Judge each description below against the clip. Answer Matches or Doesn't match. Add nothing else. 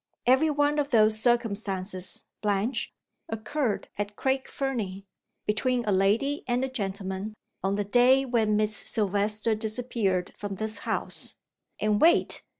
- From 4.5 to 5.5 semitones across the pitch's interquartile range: Doesn't match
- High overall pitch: Matches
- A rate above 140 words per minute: Doesn't match